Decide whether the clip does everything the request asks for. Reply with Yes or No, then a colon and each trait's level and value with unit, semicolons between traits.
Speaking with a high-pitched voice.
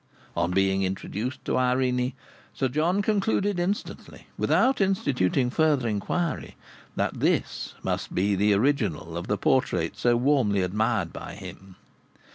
No: low, 125 Hz